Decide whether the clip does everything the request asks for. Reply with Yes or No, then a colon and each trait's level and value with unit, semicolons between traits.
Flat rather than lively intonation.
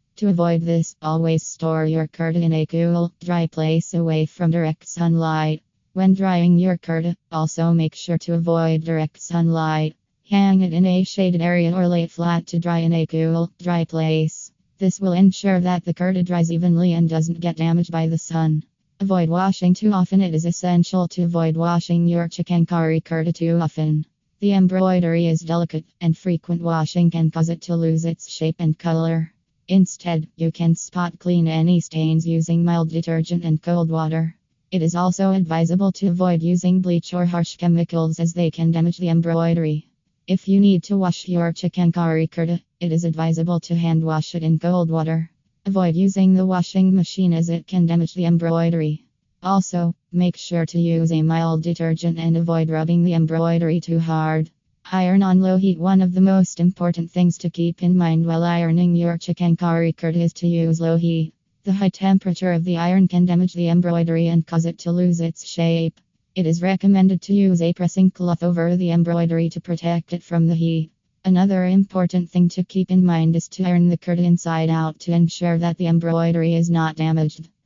Yes: narrow, 1.4 semitones